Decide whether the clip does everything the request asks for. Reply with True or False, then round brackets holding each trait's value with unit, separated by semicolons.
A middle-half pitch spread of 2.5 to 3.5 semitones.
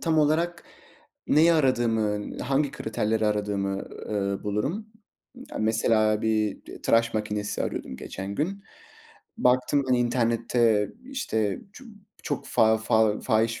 False (4.4 semitones)